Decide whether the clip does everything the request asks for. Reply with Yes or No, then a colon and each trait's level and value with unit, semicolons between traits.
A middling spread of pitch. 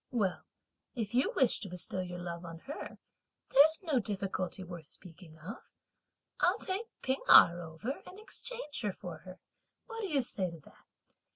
No: wide, 7.9 semitones